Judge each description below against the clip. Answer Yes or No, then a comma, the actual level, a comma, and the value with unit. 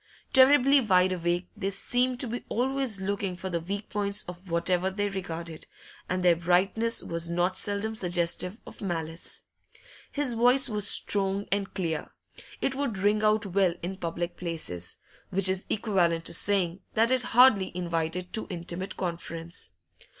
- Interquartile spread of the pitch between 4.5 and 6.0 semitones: No, average, 3.7 semitones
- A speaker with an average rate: Yes, average, 155 wpm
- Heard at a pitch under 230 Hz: Yes, high, 190 Hz